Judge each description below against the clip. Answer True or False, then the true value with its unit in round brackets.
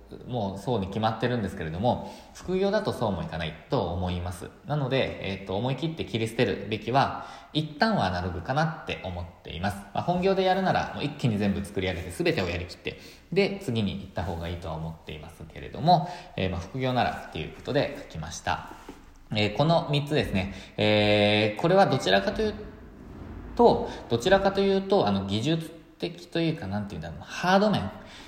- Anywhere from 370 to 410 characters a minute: True (405 characters per minute)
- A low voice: True (115 Hz)